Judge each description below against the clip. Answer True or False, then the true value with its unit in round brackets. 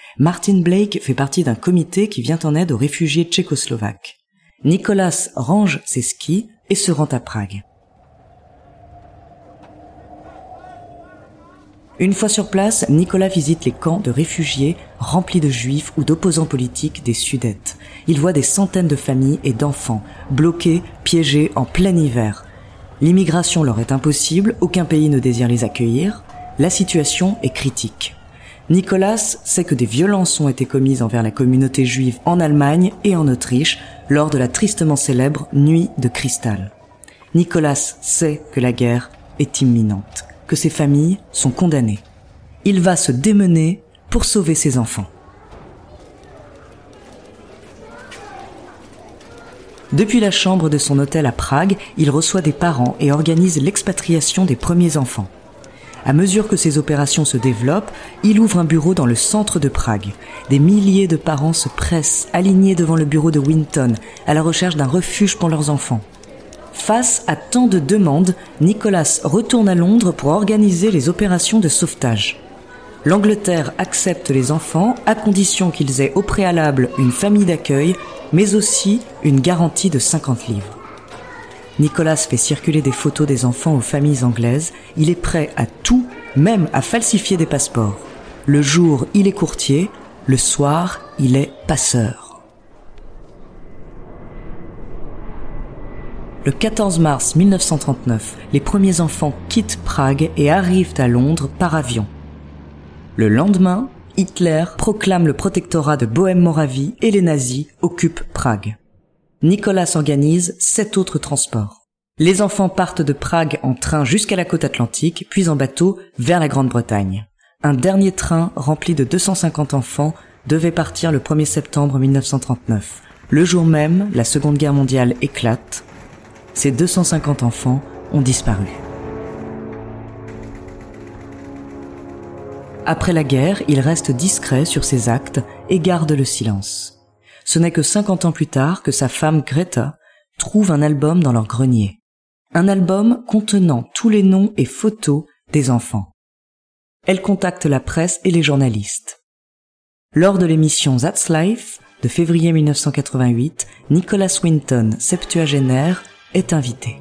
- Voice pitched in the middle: True (150 Hz)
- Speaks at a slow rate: True (140 wpm)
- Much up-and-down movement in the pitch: True (5.9 semitones)